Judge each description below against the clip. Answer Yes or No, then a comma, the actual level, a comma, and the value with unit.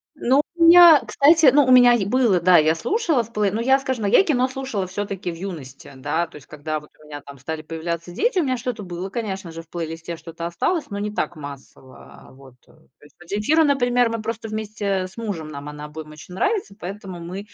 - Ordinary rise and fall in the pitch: No, wide, 7.2 semitones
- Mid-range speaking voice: No, high, 195 Hz